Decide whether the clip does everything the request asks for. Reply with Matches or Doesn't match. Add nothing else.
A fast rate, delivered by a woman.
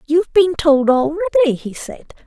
Doesn't match